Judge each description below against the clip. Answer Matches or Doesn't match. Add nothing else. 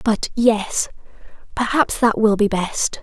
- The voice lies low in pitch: Doesn't match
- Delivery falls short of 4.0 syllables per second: Matches